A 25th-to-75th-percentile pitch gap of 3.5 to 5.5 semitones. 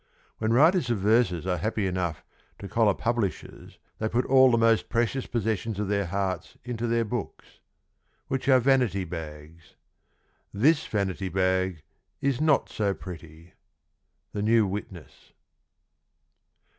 Yes: average, 4.2 semitones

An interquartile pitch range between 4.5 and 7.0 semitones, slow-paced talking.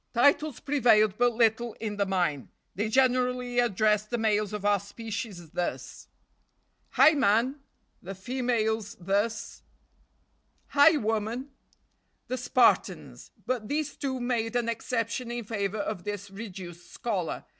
No: average, 3.3 semitones; slow, 125 wpm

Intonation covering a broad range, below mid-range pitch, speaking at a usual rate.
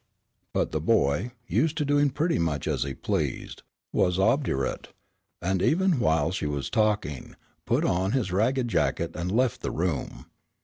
Yes: wide, 8.0 semitones; very low, 95 Hz; average, 160 wpm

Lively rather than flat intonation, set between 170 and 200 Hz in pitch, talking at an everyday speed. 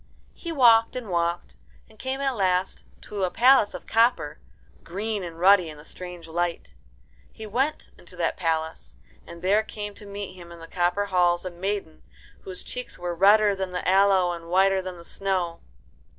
No: average, 3.1 semitones; medium, 185 Hz; average, 180 wpm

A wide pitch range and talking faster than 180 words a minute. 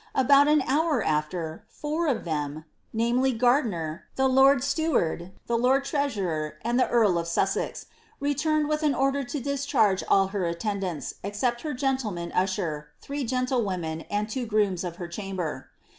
No: wide, 7.4 semitones; average, 160 wpm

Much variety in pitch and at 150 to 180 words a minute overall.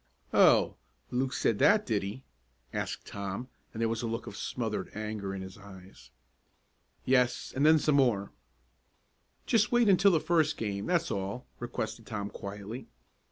Yes: wide, 6.1 semitones; average, 160 wpm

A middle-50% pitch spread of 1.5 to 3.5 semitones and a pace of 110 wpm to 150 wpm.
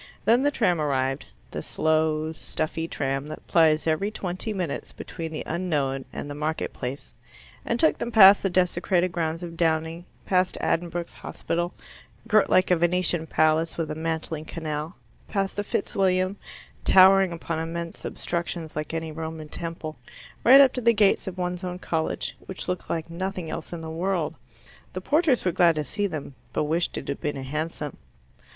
No: average, 2.8 semitones; average, 175 wpm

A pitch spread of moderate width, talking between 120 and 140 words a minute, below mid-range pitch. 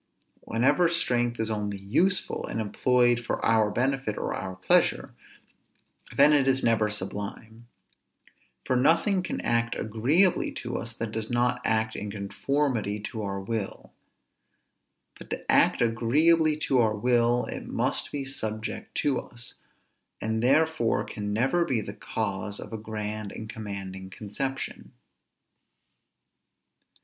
Yes: average, 3.9 semitones; slow, 135 wpm; low, 115 Hz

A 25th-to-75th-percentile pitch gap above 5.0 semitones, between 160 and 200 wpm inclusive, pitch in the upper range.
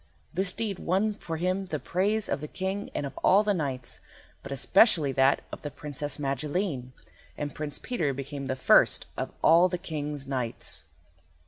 No: wide, 5.4 semitones; average, 175 wpm; medium, 150 Hz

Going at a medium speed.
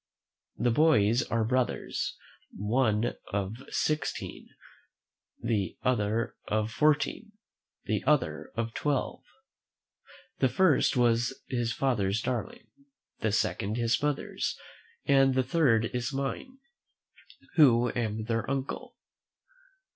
No: slow, 100 wpm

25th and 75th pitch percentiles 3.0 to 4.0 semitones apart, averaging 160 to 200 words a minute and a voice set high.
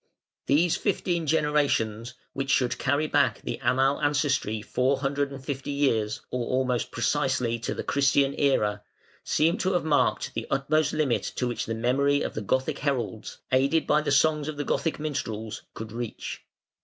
No: average, 3.3 semitones; average, 170 wpm; low, 135 Hz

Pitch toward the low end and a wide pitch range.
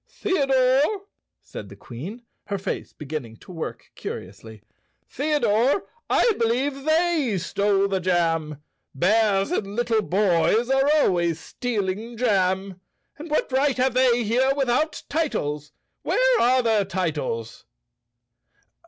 No: high, 215 Hz; wide, 6.9 semitones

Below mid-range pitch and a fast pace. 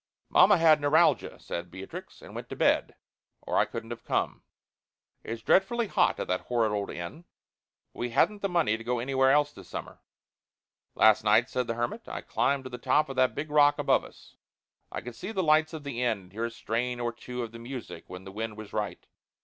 Yes: low, 125 Hz; fast, 220 wpm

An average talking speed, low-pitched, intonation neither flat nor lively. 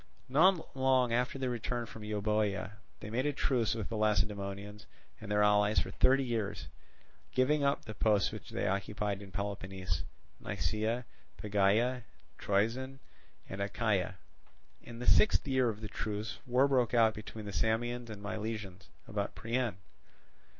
Yes: average, 145 wpm; low, 110 Hz; average, 3.1 semitones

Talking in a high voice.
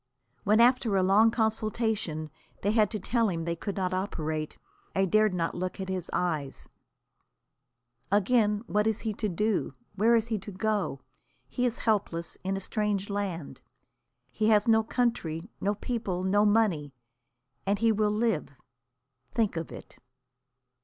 Yes: high, 205 Hz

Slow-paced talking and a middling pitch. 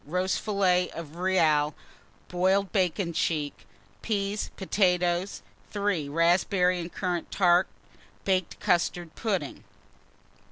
Yes: slow, 95 wpm; medium, 180 Hz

